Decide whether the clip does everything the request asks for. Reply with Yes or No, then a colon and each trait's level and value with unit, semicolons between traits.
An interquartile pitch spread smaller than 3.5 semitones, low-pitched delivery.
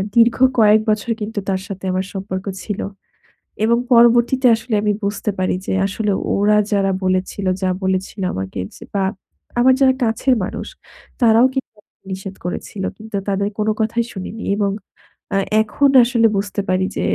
No: average, 3.0 semitones; high, 210 Hz